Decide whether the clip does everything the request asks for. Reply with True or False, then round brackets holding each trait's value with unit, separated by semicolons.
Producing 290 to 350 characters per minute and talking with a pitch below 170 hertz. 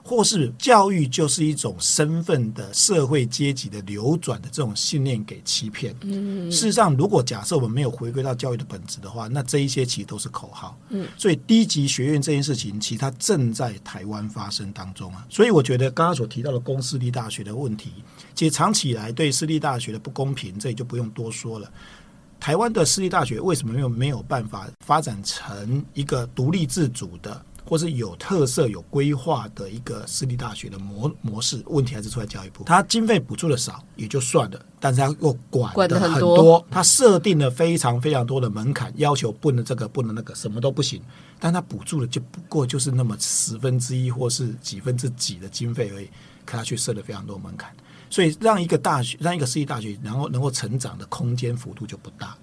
True (325 characters per minute; 135 Hz)